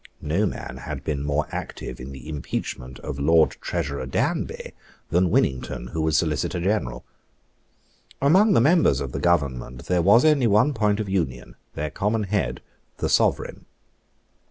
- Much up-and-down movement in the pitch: Yes, wide, 7.5 semitones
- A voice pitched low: Yes, very low, 80 Hz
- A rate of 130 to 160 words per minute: Yes, average, 155 wpm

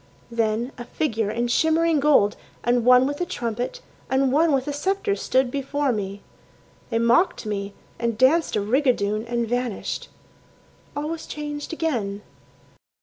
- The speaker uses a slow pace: No, average, 145 wpm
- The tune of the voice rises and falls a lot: No, average, 4.5 semitones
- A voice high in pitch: Yes, very high, 250 Hz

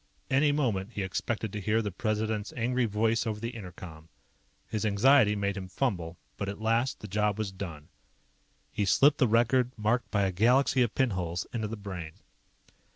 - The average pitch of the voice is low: Yes, low, 105 Hz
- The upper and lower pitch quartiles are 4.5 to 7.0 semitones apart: No, average, 3.2 semitones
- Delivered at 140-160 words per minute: No, average, 180 wpm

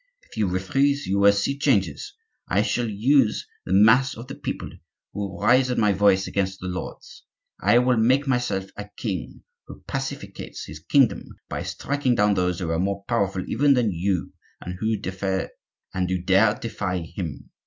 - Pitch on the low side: Yes, low, 100 Hz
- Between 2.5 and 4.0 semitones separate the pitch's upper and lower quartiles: No, average, 4.6 semitones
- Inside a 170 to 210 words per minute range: Yes, average, 175 wpm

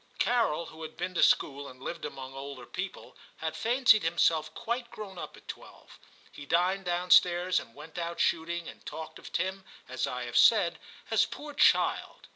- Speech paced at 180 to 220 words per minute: Yes, average, 185 wpm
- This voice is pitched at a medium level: Yes, medium, 170 Hz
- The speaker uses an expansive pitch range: No, average, 3.9 semitones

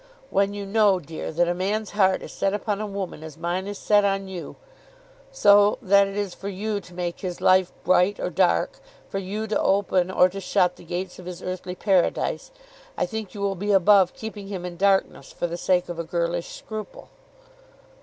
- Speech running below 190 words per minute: No, fast, 205 wpm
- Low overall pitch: No, high, 190 Hz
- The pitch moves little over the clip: Yes, narrow, 2.2 semitones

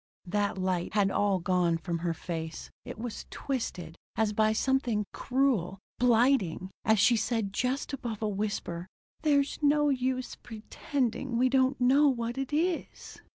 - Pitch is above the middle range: Yes, high, 225 Hz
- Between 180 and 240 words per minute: No, average, 150 wpm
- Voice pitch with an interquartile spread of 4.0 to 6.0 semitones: Yes, wide, 5.4 semitones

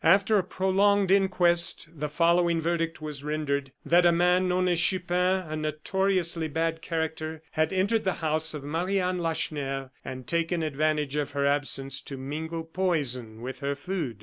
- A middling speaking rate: Yes, average, 165 wpm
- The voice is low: No, medium, 165 Hz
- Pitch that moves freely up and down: No, average, 3.5 semitones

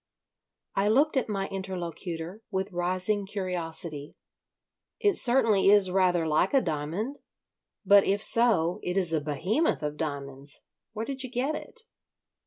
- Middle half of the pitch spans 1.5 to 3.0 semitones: No, average, 4.9 semitones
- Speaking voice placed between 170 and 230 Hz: Yes, high, 190 Hz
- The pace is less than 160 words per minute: Yes, average, 140 wpm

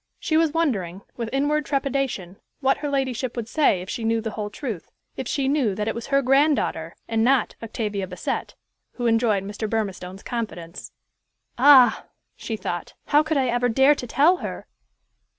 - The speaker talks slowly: No, average, 175 wpm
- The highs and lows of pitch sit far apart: No, average, 4.8 semitones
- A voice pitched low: No, high, 240 Hz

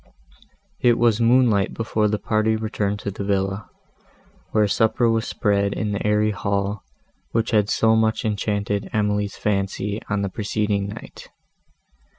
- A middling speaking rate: Yes, average, 145 wpm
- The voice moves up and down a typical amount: No, narrow, 1.6 semitones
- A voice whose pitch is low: Yes, low, 105 Hz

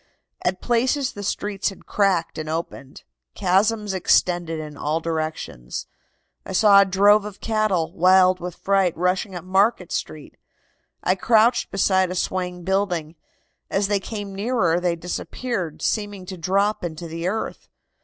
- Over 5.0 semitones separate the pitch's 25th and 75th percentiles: No, average, 3.1 semitones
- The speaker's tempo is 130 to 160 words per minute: Yes, average, 145 wpm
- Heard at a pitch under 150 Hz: No, medium, 185 Hz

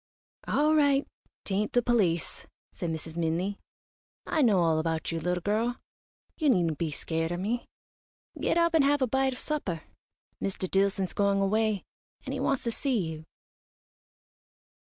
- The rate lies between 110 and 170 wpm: Yes, average, 160 wpm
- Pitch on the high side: Yes, high, 200 Hz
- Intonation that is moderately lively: No, wide, 6.9 semitones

